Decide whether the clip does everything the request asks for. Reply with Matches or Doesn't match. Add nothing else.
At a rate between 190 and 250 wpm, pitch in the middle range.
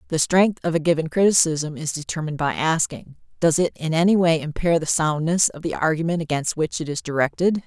Matches